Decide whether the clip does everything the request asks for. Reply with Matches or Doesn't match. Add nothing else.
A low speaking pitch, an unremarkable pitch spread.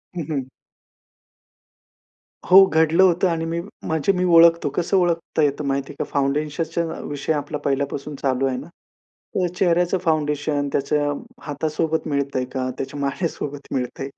Doesn't match